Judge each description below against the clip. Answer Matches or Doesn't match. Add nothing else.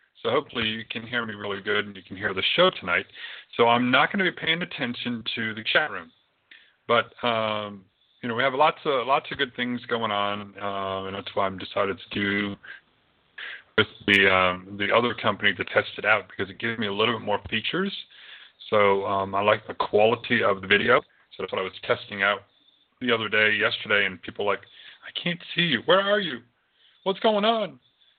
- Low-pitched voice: Matches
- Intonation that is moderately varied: Matches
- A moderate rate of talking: Doesn't match